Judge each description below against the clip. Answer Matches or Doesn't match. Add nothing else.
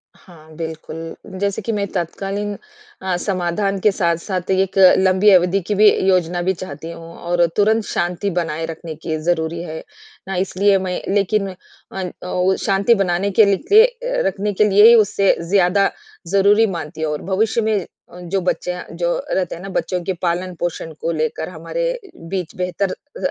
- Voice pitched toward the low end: Doesn't match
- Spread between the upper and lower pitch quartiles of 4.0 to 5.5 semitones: Doesn't match